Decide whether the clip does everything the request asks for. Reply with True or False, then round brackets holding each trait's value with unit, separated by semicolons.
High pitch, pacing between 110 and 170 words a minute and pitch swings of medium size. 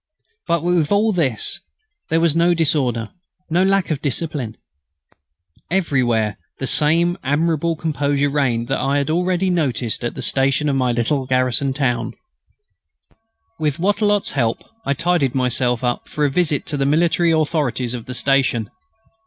False (145 Hz; 150 wpm; 4.7 semitones)